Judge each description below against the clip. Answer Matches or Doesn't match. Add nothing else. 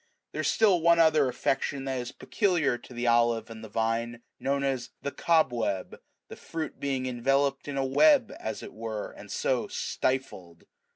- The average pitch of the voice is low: Matches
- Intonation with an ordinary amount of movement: Matches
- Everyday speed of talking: Matches